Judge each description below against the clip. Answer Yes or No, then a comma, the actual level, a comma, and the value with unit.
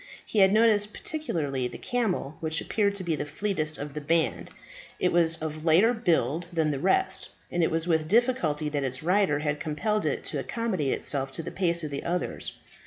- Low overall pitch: No, medium, 165 Hz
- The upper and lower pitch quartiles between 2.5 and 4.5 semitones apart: No, average, 5.1 semitones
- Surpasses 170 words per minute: Yes, average, 200 wpm